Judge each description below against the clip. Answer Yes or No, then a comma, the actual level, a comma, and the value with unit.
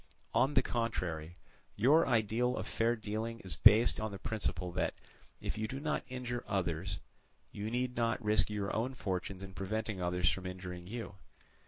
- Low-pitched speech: Yes, low, 110 Hz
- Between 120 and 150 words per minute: No, average, 170 wpm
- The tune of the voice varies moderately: Yes, average, 4.2 semitones